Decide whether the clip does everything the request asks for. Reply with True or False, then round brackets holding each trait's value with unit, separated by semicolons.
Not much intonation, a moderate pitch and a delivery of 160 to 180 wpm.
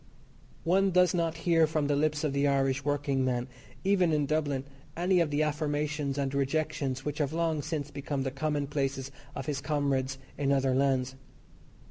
True (2.3 semitones; 145 Hz; 165 wpm)